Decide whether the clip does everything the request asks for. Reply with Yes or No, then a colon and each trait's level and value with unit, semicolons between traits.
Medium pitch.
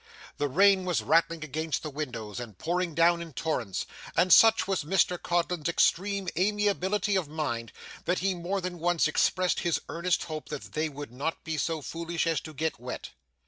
Yes: medium, 165 Hz